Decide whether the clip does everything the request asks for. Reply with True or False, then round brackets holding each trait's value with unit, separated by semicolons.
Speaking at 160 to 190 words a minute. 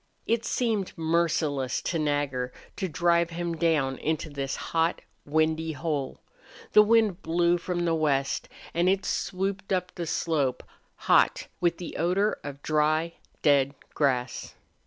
False (135 wpm)